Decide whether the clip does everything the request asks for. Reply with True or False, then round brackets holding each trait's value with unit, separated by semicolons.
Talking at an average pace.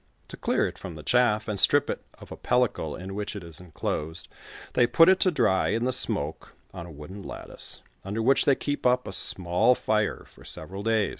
False (215 wpm)